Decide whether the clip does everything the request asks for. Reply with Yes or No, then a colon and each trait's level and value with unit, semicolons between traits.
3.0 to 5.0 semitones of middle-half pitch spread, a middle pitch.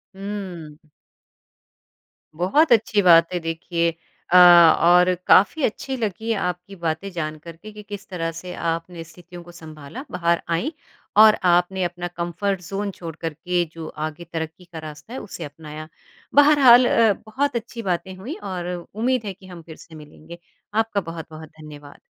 Yes: average, 3.9 semitones; medium, 175 Hz